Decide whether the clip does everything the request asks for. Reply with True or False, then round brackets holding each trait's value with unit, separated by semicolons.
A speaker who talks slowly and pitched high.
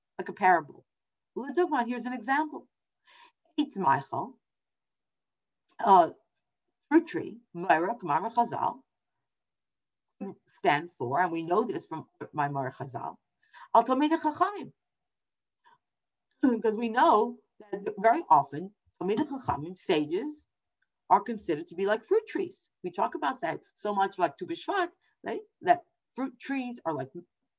True (100 wpm; 245 Hz)